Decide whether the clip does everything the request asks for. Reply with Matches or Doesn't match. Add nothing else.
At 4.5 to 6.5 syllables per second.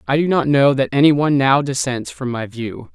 Matches